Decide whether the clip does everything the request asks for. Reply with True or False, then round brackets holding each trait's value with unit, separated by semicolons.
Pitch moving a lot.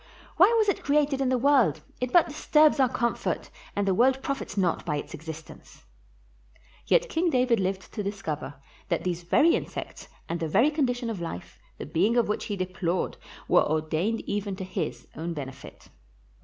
True (7.8 semitones)